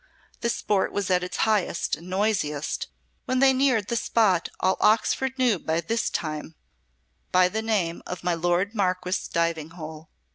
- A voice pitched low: No, medium, 185 Hz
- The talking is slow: No, average, 160 wpm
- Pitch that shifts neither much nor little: Yes, average, 4.7 semitones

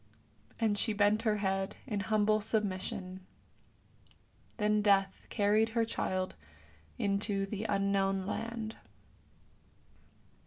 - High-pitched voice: Yes, high, 205 Hz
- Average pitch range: No, narrow, 1.8 semitones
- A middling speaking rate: No, slow, 105 wpm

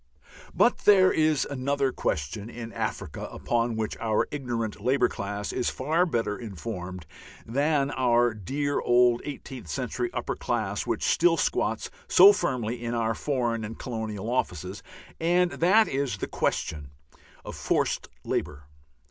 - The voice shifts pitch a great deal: No, average, 4.6 semitones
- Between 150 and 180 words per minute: No, average, 140 wpm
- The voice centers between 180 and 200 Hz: No, low, 120 Hz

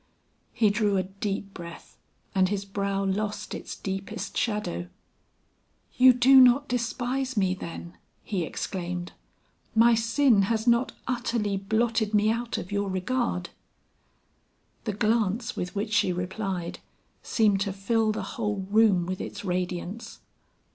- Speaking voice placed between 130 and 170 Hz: No, high, 205 Hz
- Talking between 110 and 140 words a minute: Yes, slow, 135 wpm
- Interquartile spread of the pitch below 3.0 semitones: No, average, 3.4 semitones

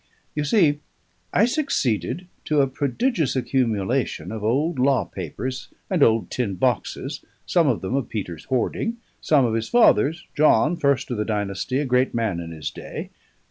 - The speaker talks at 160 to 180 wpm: Yes, average, 165 wpm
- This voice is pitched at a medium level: No, low, 130 Hz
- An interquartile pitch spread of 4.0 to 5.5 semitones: Yes, average, 5.2 semitones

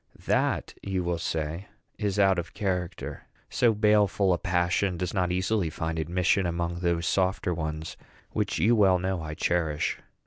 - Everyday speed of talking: Yes, average, 160 wpm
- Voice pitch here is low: Yes, very low, 90 Hz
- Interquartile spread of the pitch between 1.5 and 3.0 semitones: Yes, narrow, 2.4 semitones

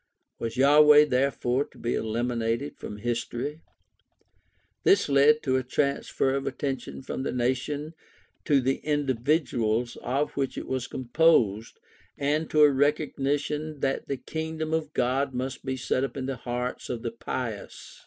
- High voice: No, low, 135 Hz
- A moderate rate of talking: Yes, average, 150 wpm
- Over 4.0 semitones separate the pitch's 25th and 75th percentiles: No, average, 3.1 semitones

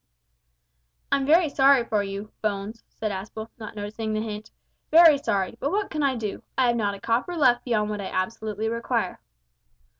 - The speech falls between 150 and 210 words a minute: Yes, average, 180 wpm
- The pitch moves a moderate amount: Yes, average, 4.2 semitones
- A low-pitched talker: No, high, 225 Hz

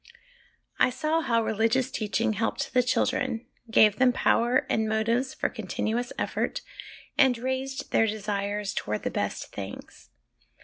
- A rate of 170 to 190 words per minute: No, slow, 135 wpm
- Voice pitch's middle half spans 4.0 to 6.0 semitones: No, average, 2.9 semitones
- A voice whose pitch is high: Yes, high, 230 Hz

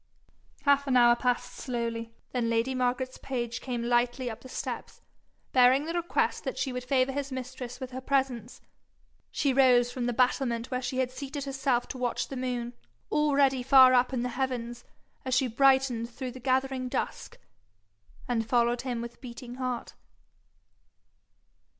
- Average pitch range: No, narrow, 1.7 semitones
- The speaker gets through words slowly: No, average, 160 wpm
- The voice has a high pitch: Yes, very high, 255 Hz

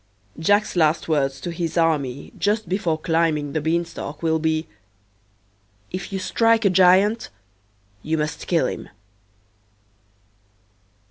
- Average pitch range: Yes, average, 3.2 semitones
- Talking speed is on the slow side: Yes, slow, 120 wpm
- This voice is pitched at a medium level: Yes, medium, 165 Hz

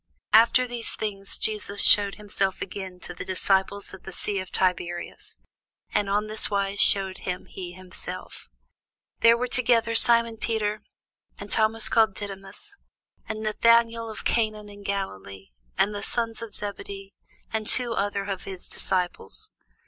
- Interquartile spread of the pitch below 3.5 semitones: Yes, average, 2.7 semitones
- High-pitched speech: Yes, high, 205 Hz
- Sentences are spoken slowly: No, average, 145 wpm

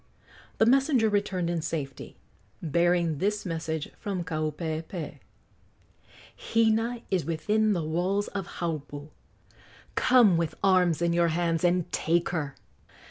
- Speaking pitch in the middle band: Yes, medium, 175 Hz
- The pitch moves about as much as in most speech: Yes, average, 4.0 semitones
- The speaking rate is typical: No, slow, 120 wpm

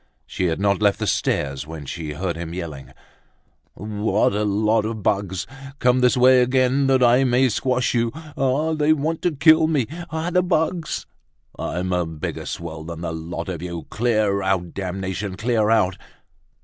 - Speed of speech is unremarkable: Yes, average, 160 wpm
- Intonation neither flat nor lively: No, wide, 6.5 semitones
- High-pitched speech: No, low, 105 Hz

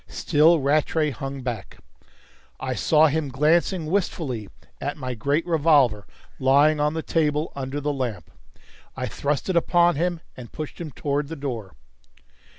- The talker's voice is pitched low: No, medium, 145 Hz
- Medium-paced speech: Yes, average, 150 wpm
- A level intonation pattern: No, average, 3.2 semitones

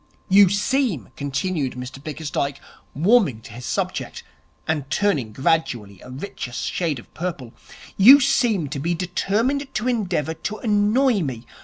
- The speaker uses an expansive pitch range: Yes, wide, 7.4 semitones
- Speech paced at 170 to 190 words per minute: No, average, 140 wpm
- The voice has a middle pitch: Yes, medium, 170 Hz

